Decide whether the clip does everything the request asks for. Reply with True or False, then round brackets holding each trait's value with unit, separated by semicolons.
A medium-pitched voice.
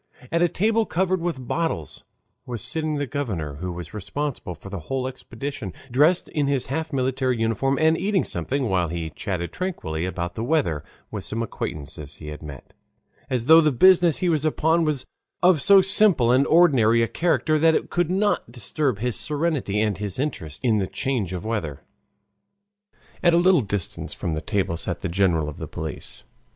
False (130 Hz)